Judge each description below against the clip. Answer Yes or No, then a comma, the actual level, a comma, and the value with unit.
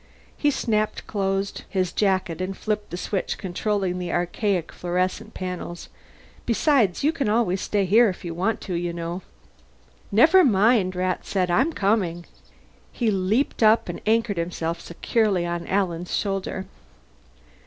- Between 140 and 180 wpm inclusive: Yes, average, 145 wpm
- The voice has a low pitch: No, high, 190 Hz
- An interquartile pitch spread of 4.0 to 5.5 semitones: No, average, 3.4 semitones